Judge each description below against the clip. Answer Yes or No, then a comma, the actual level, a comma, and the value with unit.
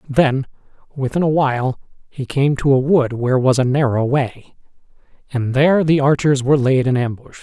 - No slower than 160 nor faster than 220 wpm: Yes, average, 180 wpm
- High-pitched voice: No, low, 135 Hz